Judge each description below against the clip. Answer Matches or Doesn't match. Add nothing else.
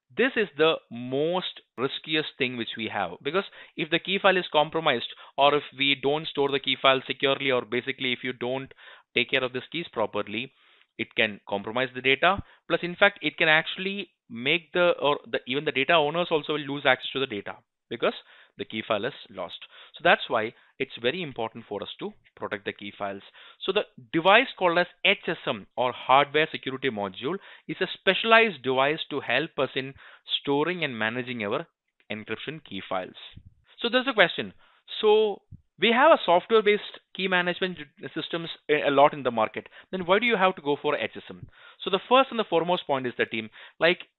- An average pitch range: Doesn't match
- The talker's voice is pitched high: Doesn't match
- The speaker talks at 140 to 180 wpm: Doesn't match